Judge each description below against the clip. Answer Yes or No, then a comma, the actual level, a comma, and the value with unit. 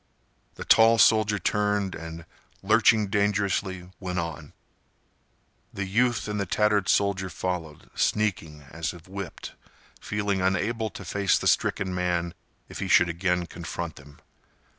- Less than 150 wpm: Yes, slow, 135 wpm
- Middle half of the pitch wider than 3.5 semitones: No, average, 3.1 semitones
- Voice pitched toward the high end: No, very low, 95 Hz